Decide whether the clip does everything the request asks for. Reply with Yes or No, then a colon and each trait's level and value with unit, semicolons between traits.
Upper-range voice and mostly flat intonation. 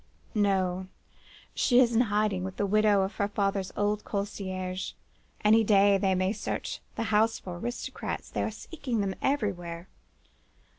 Yes: high, 200 Hz; narrow, 2.2 semitones